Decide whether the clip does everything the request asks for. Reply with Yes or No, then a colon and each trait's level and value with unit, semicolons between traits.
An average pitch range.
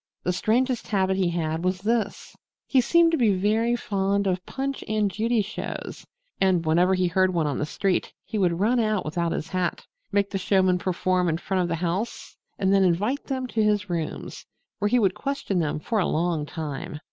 Yes: average, 3.6 semitones